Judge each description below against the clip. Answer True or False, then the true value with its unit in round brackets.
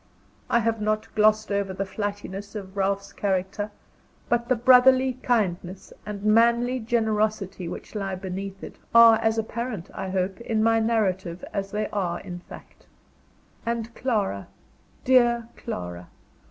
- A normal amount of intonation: True (3.0 semitones)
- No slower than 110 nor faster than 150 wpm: True (140 wpm)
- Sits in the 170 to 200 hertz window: False (210 Hz)